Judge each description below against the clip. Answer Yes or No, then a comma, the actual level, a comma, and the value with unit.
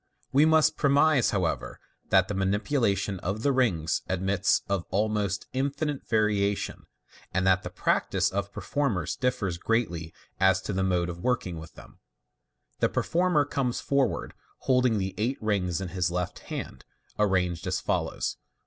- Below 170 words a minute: Yes, average, 145 wpm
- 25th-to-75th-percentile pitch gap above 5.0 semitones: Yes, wide, 5.5 semitones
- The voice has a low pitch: Yes, low, 100 Hz